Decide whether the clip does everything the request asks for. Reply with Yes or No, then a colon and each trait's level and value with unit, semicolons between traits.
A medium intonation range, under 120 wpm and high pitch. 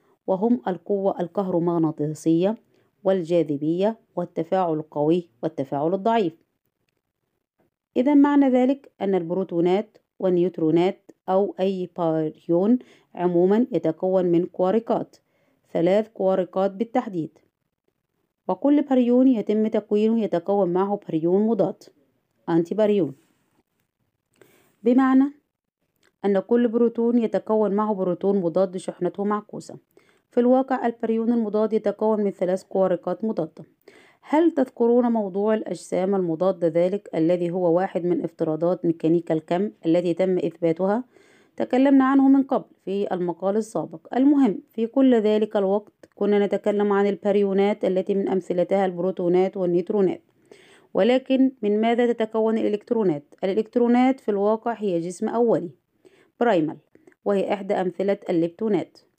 Yes: average, 4.4 semitones; average, 105 wpm; high, 200 Hz